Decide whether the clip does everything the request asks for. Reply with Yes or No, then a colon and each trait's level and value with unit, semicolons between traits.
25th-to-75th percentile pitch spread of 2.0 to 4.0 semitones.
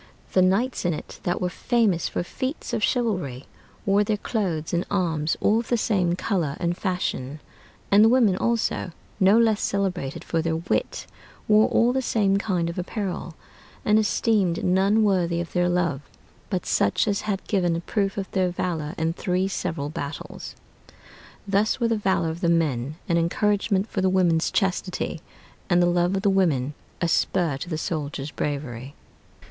Yes: average, 3.5 semitones